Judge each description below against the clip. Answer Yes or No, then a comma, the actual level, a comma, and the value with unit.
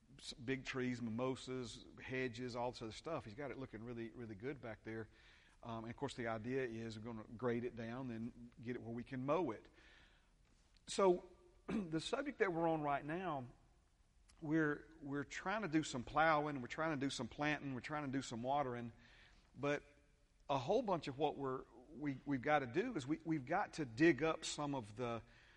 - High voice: No, low, 130 Hz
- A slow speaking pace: No, fast, 205 wpm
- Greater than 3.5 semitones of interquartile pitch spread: Yes, average, 4.0 semitones